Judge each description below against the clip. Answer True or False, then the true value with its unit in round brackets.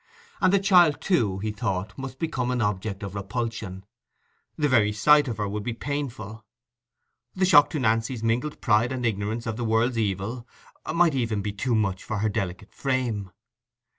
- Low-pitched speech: True (115 Hz)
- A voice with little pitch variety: False (3.9 semitones)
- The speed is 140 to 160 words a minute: False (175 wpm)